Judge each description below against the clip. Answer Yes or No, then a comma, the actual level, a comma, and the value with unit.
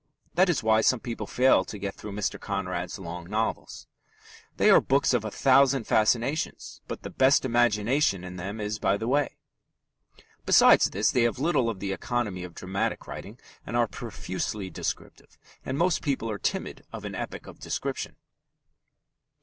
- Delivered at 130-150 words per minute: No, average, 170 wpm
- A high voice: No, low, 110 Hz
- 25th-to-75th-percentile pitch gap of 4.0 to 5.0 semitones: Yes, average, 4.7 semitones